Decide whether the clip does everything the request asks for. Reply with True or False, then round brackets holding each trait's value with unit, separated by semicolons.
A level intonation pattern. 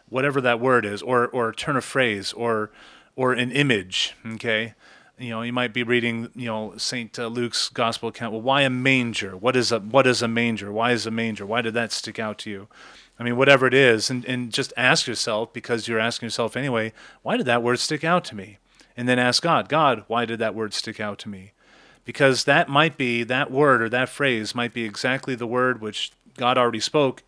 True (2.2 semitones)